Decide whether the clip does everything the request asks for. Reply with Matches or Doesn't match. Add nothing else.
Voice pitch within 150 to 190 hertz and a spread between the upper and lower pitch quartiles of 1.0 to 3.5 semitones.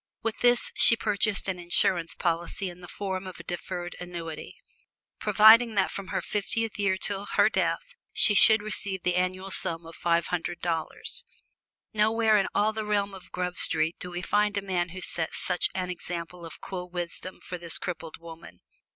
Matches